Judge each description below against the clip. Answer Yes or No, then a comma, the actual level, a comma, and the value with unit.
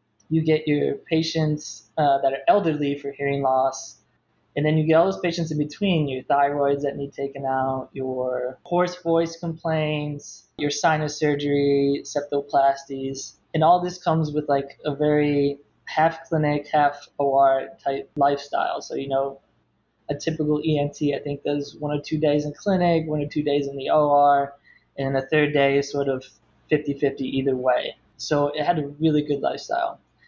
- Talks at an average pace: Yes, average, 175 wpm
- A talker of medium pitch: Yes, medium, 145 Hz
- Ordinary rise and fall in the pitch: No, narrow, 1.8 semitones